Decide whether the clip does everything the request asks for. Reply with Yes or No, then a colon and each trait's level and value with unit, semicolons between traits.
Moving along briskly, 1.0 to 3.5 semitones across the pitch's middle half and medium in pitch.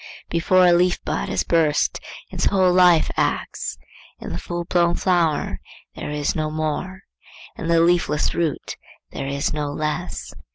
No: average, 155 wpm; average, 2.8 semitones; medium, 165 Hz